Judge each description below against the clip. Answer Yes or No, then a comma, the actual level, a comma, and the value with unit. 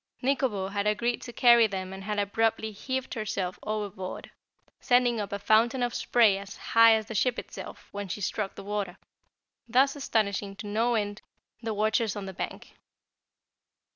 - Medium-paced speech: Yes, average, 165 wpm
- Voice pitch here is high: Yes, high, 215 Hz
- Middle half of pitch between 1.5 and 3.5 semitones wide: Yes, average, 2.8 semitones